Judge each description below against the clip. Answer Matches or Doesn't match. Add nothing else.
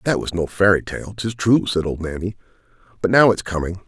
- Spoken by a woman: Doesn't match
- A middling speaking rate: Doesn't match